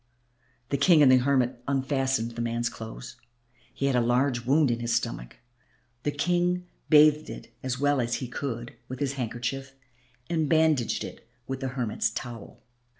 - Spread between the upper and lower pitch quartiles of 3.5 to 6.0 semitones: No, average, 3.0 semitones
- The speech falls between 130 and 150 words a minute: No, average, 165 wpm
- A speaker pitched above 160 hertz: No, low, 130 Hz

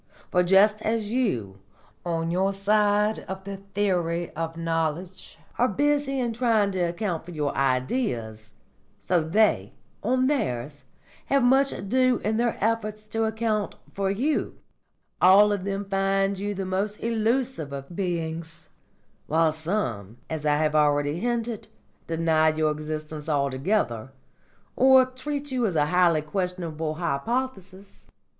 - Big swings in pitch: Yes, wide, 5.7 semitones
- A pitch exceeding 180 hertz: Yes, high, 190 Hz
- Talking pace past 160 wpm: No, slow, 135 wpm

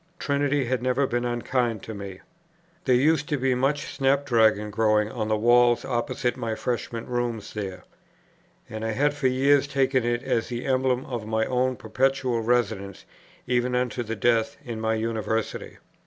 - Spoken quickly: No, average, 165 wpm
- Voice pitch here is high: No, low, 120 Hz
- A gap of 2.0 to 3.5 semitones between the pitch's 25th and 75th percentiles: Yes, average, 2.8 semitones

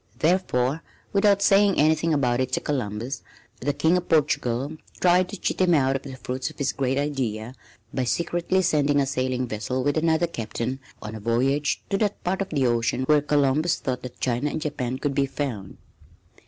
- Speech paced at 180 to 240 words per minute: Yes, average, 190 wpm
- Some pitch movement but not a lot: Yes, average, 4.1 semitones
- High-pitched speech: No, medium, 140 Hz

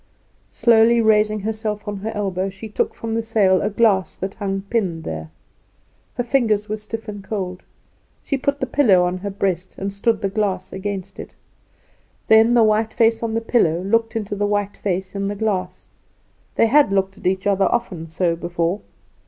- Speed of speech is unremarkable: Yes, average, 185 wpm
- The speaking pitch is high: Yes, high, 205 Hz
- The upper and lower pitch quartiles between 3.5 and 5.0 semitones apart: No, average, 2.7 semitones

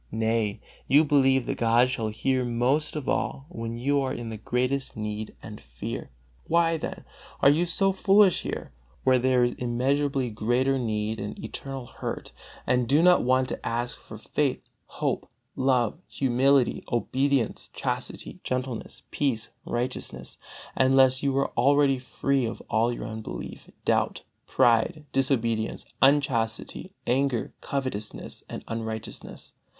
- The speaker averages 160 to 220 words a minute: No, slow, 135 wpm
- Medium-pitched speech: No, low, 130 Hz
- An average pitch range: Yes, average, 3.2 semitones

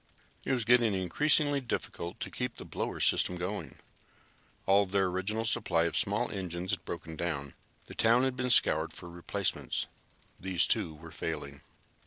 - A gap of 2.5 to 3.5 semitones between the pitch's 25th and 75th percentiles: No, average, 5.3 semitones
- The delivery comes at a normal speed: Yes, average, 165 wpm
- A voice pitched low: Yes, very low, 95 Hz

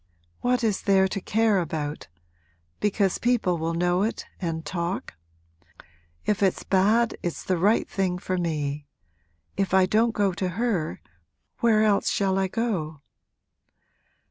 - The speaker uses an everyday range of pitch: Yes, average, 3.6 semitones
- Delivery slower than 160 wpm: Yes, average, 140 wpm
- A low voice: No, high, 190 Hz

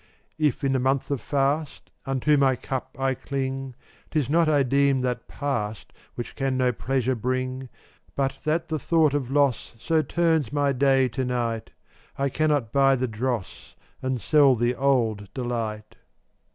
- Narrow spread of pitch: Yes, narrow, 2.3 semitones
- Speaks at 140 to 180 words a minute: Yes, average, 165 wpm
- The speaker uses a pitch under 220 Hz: Yes, low, 135 Hz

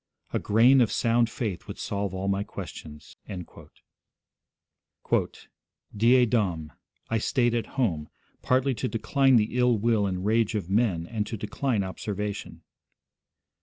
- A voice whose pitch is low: Yes, low, 110 Hz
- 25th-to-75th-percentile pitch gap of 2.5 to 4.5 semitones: Yes, average, 3.6 semitones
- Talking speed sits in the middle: No, slow, 130 wpm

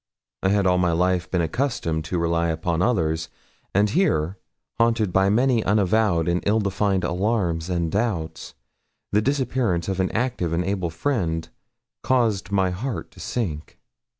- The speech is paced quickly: No, average, 150 wpm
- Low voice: Yes, very low, 95 Hz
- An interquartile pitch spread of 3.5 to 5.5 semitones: Yes, average, 4.6 semitones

